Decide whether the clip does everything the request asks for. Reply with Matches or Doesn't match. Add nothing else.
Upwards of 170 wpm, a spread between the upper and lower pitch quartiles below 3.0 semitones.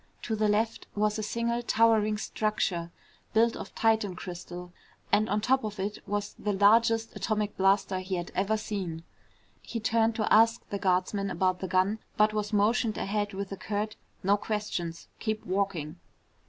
Doesn't match